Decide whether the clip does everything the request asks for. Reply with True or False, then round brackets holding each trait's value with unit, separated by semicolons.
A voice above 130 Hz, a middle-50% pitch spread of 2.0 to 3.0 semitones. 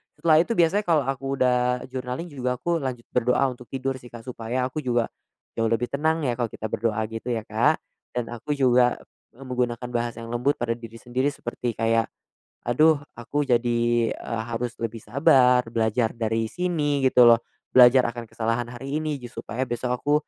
False (125 Hz; 2.5 semitones)